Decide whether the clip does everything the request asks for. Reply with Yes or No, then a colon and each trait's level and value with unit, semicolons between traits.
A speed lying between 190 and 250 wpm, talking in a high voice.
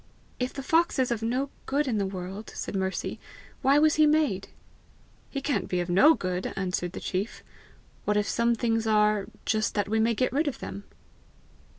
Yes: average, 195 wpm; high, 220 Hz